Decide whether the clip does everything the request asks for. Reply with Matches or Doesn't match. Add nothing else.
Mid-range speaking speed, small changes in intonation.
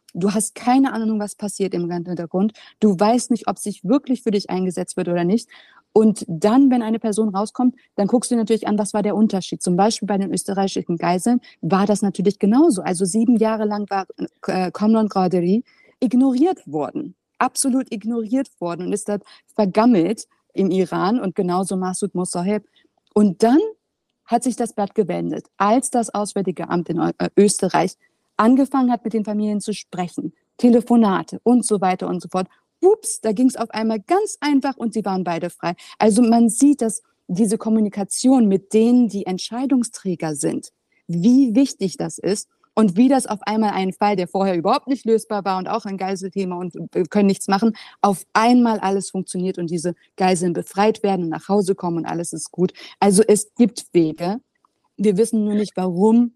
Doesn't match